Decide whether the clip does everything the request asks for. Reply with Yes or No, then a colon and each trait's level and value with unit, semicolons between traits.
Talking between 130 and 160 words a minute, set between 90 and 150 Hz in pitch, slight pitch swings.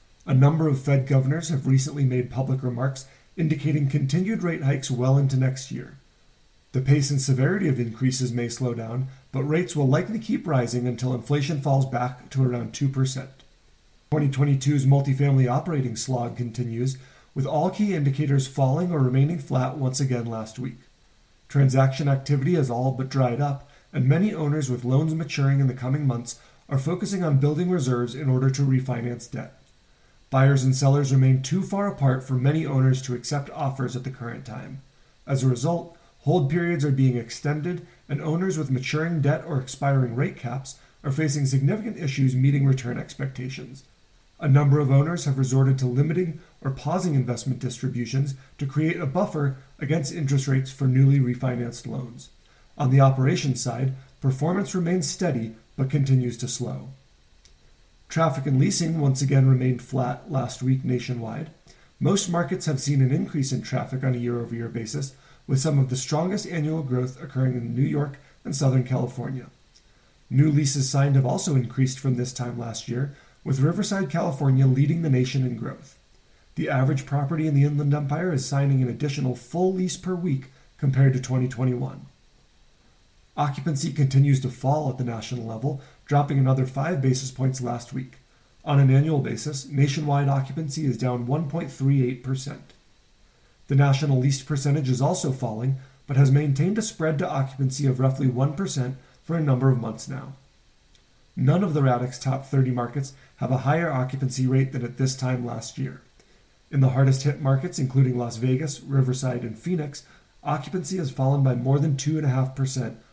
No: average, 170 wpm; low, 135 Hz; narrow, 2.2 semitones